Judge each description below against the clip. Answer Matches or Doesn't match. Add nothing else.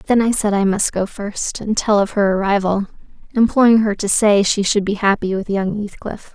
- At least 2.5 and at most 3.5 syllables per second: Doesn't match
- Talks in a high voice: Matches